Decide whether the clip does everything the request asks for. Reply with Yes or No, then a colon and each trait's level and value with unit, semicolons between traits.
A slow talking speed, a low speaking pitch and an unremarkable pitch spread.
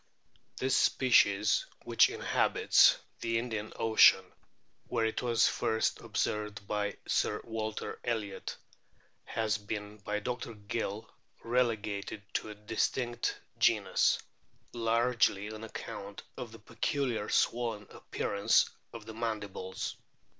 No: slow, 110 wpm; low, 110 Hz; narrow, 2.0 semitones